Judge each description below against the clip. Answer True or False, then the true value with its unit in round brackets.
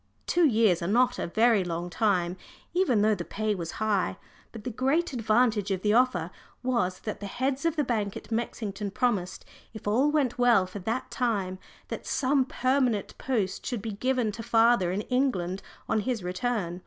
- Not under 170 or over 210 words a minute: True (185 wpm)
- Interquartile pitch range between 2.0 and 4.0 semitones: False (4.6 semitones)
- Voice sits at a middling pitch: False (220 Hz)